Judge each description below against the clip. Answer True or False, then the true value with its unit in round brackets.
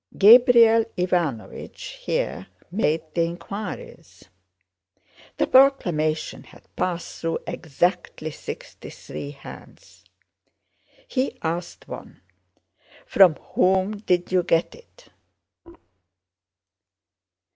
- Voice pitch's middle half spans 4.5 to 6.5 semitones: True (4.9 semitones)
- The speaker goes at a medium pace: False (80 wpm)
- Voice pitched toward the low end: False (180 Hz)